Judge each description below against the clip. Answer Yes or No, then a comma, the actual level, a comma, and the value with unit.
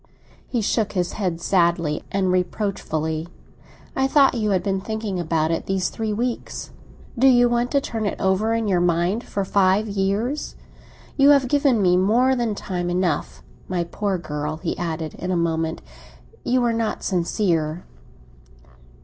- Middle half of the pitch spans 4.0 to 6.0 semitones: Yes, average, 4.7 semitones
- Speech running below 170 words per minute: Yes, average, 160 wpm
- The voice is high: Yes, high, 195 Hz